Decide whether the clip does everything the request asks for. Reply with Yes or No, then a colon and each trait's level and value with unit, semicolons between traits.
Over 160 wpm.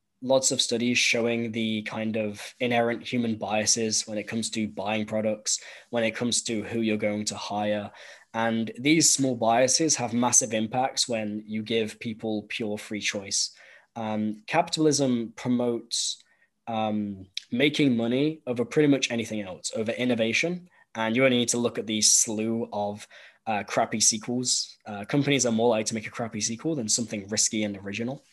Yes: average, 170 wpm